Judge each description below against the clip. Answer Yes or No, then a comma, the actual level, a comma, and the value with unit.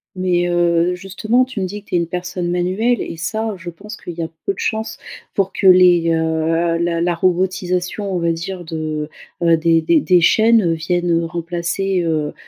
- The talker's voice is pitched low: No, medium, 175 Hz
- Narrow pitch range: Yes, narrow, 2.3 semitones